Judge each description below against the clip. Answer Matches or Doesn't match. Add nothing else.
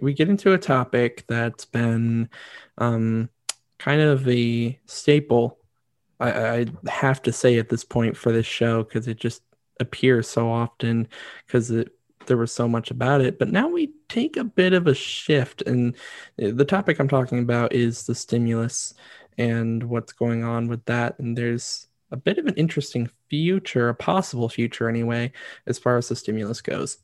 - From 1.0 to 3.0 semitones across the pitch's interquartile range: Matches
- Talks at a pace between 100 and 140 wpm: Doesn't match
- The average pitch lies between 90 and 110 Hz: Doesn't match